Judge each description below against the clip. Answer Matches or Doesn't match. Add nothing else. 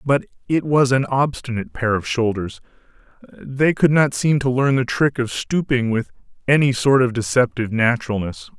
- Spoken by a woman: Doesn't match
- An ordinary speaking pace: Matches